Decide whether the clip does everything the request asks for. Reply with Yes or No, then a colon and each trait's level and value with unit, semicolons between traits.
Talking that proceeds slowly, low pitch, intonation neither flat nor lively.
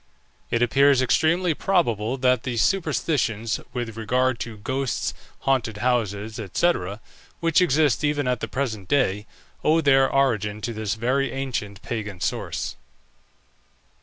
Yes: slow, 130 wpm; low, 125 Hz; average, 4.1 semitones